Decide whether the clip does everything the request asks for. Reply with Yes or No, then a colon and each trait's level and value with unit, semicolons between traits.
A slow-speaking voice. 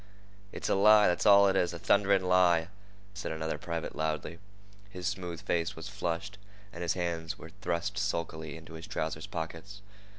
No: average, 165 wpm